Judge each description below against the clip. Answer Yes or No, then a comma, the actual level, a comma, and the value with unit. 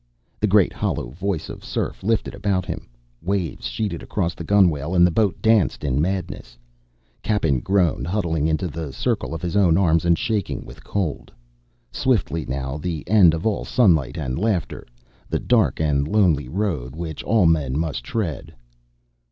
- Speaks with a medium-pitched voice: No, very low, 85 Hz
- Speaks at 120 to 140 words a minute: No, average, 165 wpm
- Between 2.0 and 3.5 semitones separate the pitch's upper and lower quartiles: No, average, 4.8 semitones